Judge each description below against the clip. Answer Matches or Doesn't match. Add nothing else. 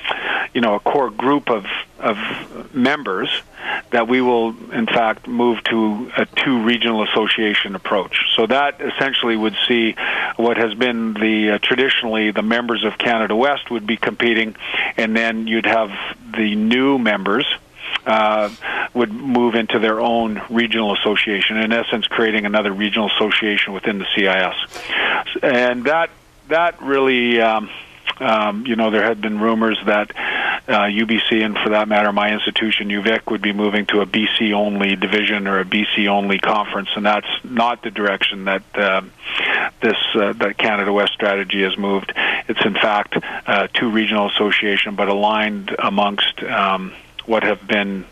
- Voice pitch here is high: Doesn't match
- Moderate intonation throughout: Doesn't match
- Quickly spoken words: Doesn't match